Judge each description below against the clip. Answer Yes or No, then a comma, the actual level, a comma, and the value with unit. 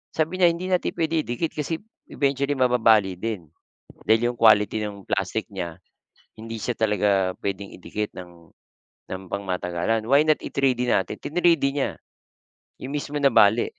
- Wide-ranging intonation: Yes, wide, 6.1 semitones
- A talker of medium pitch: No, low, 115 Hz